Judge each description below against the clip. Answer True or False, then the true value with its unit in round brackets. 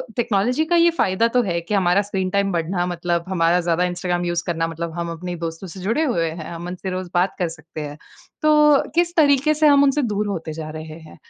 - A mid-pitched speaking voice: True (180 Hz)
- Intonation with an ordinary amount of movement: False (5.9 semitones)